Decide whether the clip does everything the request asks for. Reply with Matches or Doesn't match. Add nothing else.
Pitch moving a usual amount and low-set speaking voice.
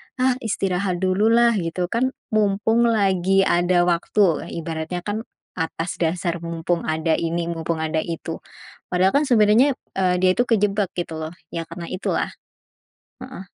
Doesn't match